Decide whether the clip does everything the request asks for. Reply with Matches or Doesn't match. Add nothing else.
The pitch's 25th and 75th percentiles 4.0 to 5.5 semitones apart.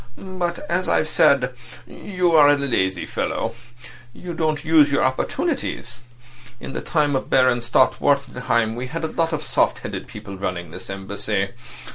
Matches